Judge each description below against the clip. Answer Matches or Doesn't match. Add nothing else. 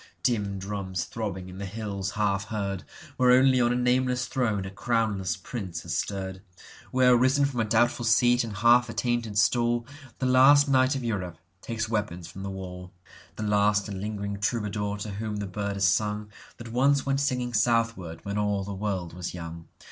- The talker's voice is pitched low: Matches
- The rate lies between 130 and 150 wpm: Doesn't match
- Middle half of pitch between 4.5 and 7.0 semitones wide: Doesn't match